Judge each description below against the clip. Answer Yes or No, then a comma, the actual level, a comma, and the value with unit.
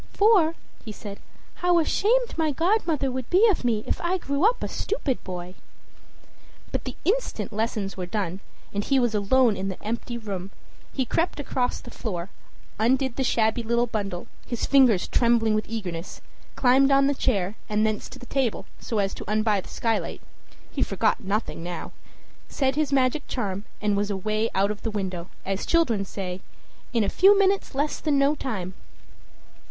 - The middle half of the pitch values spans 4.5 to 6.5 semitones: Yes, wide, 5.5 semitones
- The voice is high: Yes, high, 230 Hz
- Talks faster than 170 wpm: Yes, average, 180 wpm